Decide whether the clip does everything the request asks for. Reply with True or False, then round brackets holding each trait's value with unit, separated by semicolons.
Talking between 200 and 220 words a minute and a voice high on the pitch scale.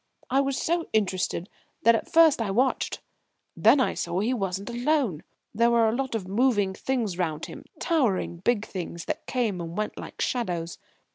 False (180 wpm; 220 Hz)